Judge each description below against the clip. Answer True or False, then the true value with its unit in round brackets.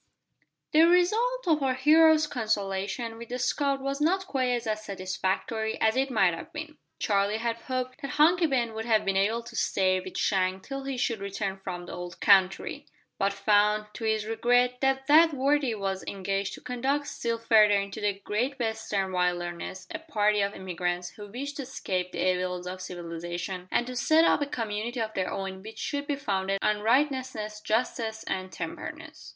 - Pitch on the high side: True (220 Hz)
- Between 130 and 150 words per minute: False (185 wpm)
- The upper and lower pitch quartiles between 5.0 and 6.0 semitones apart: True (5.5 semitones)